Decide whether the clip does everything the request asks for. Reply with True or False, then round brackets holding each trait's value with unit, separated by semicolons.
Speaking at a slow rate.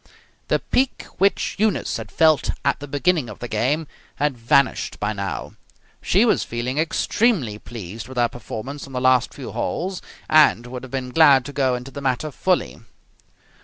False (175 wpm)